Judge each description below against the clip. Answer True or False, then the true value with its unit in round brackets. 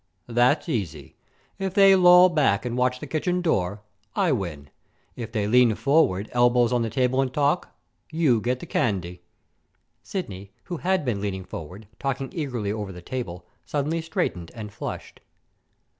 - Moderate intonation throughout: False (7.3 semitones)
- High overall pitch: False (125 Hz)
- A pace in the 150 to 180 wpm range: True (160 wpm)